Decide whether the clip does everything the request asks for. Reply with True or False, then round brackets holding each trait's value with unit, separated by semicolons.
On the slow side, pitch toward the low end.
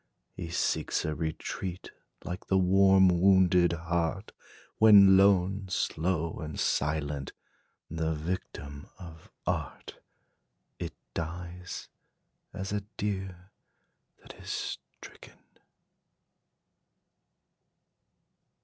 True (85 wpm; 90 Hz)